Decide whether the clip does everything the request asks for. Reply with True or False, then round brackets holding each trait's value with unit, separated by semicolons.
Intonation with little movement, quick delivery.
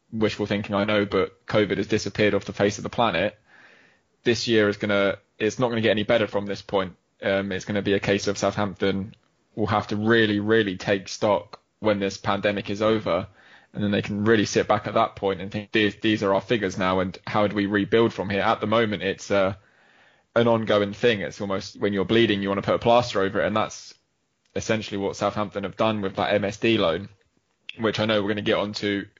True (1.6 semitones; 230 wpm)